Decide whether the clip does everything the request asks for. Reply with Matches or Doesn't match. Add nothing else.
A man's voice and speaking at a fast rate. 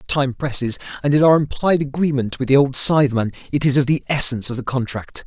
Matches